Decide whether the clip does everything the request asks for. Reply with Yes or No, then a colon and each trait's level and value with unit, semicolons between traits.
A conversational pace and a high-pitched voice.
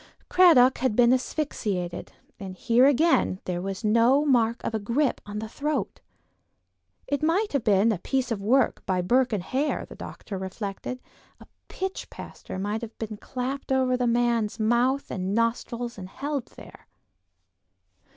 Yes: average, 160 wpm; high, 235 Hz